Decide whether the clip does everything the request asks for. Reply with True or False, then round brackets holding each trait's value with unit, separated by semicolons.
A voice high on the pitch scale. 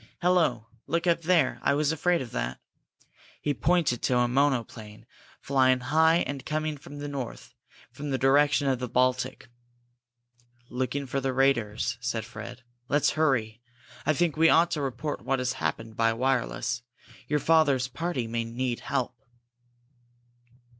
False (135 Hz)